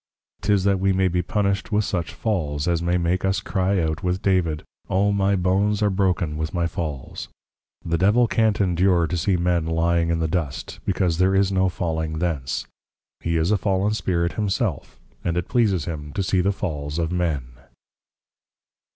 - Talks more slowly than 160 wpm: No, average, 185 wpm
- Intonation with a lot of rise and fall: No, average, 2.8 semitones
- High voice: No, very low, 90 Hz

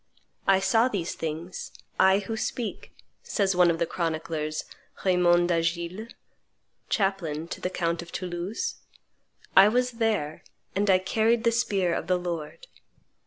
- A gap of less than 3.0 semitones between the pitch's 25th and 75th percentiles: No, average, 3.7 semitones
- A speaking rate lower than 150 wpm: Yes, average, 140 wpm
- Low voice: No, medium, 185 Hz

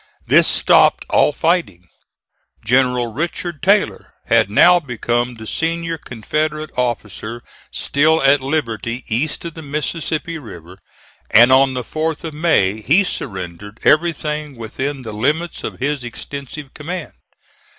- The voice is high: No, medium, 140 Hz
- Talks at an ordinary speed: No, slow, 130 wpm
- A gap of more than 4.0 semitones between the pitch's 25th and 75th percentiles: Yes, average, 5.2 semitones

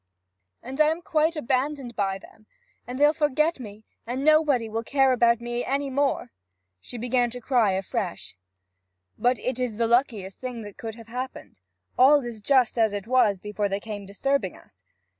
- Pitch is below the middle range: No, high, 245 Hz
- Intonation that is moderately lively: Yes, average, 3.8 semitones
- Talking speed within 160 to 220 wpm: Yes, average, 175 wpm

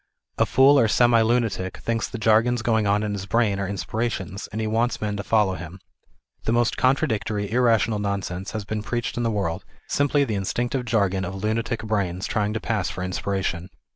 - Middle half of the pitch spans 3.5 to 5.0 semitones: No, average, 2.8 semitones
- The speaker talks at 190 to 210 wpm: Yes, average, 195 wpm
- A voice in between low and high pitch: No, low, 110 Hz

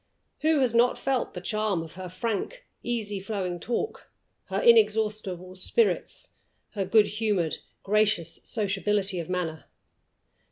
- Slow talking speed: Yes, slow, 125 wpm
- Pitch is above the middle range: Yes, high, 210 Hz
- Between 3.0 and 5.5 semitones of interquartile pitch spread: Yes, average, 3.8 semitones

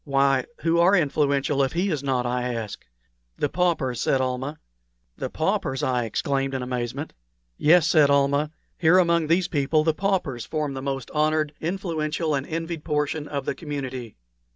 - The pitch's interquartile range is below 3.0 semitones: No, average, 3.4 semitones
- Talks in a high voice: No, medium, 145 Hz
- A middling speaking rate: Yes, average, 165 wpm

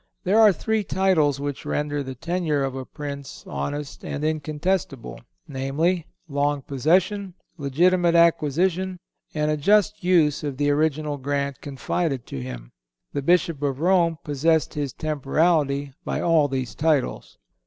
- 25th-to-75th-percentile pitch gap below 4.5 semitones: Yes, average, 3.5 semitones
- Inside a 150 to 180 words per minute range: No, average, 140 wpm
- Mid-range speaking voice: Yes, medium, 150 Hz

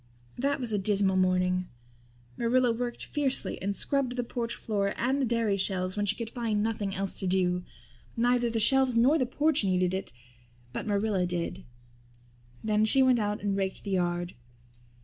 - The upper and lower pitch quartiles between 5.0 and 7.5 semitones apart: No, average, 4.2 semitones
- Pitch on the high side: Yes, high, 210 Hz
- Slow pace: No, average, 175 wpm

